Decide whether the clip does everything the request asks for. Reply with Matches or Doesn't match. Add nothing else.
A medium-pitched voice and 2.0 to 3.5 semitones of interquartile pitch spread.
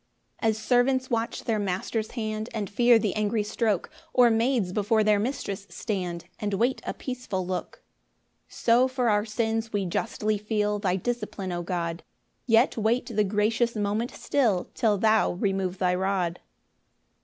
Doesn't match